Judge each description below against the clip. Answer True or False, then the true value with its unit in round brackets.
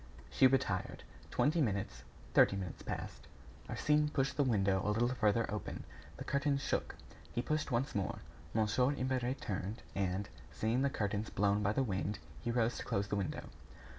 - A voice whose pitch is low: True (110 Hz)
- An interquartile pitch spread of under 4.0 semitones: False (4.8 semitones)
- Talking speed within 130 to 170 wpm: True (165 wpm)